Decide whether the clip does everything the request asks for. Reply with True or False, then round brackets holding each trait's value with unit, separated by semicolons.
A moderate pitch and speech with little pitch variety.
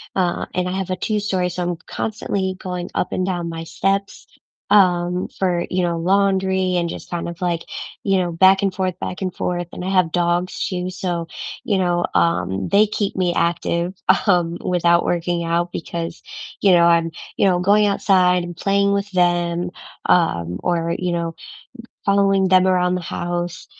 True (180 Hz; 1.7 semitones)